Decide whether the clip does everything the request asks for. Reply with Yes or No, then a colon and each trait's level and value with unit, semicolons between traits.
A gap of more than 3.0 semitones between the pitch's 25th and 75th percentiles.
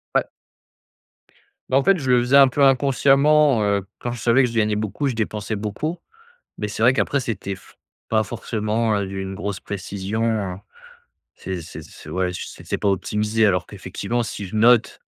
Yes: average, 3.8 semitones